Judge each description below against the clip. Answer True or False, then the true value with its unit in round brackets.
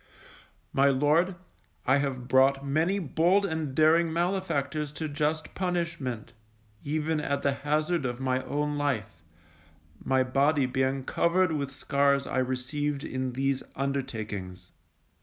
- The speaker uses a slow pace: True (125 wpm)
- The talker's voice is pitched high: False (140 Hz)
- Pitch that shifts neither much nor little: True (3.1 semitones)